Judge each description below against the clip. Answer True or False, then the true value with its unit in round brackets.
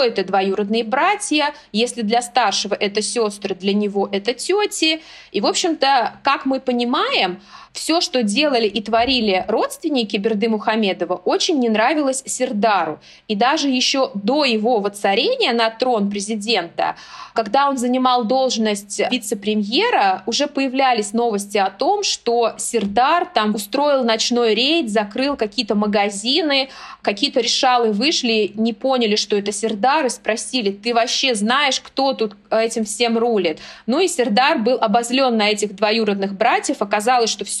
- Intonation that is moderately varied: True (3.9 semitones)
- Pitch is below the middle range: False (235 Hz)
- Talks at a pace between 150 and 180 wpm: False (140 wpm)